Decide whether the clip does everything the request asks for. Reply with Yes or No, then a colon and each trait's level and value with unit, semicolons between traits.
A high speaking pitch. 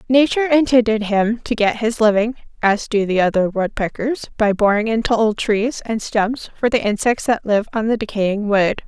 Yes: high, 220 Hz